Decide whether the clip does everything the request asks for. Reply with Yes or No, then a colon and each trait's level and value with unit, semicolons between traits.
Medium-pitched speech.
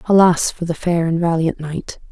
Yes: medium, 170 Hz